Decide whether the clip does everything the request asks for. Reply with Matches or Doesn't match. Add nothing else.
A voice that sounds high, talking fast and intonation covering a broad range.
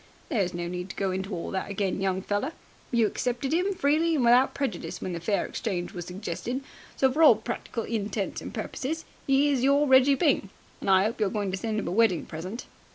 Matches